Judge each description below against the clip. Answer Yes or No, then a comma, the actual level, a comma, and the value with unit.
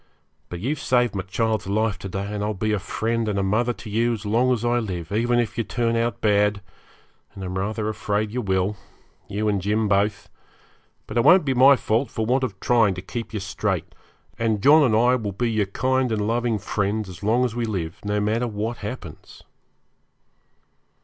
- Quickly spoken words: Yes, fast, 210 wpm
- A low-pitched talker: Yes, low, 110 Hz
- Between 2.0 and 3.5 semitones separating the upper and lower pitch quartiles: Yes, average, 2.8 semitones